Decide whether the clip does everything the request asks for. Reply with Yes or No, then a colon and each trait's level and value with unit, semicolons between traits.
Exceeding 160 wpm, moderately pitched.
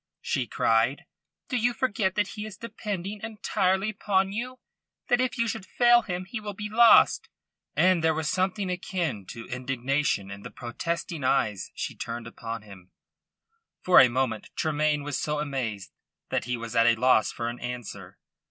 Yes: average, 170 wpm; medium, 160 Hz